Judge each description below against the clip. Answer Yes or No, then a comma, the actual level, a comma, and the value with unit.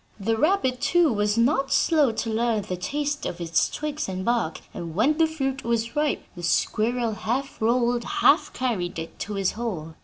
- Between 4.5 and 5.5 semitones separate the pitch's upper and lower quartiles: Yes, average, 5.2 semitones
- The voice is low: No, high, 235 Hz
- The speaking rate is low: No, average, 185 wpm